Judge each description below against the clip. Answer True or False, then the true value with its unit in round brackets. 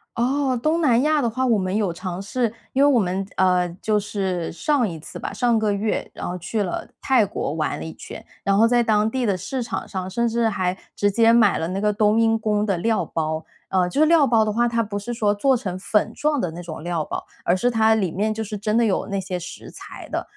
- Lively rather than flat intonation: False (4.0 semitones)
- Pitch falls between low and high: False (210 Hz)